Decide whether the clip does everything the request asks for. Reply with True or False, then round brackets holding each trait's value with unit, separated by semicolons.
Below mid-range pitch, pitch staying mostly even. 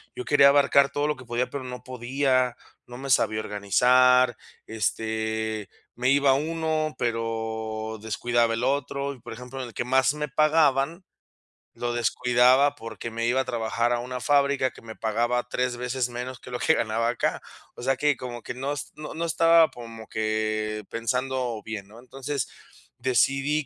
False (125 Hz; 3.2 semitones)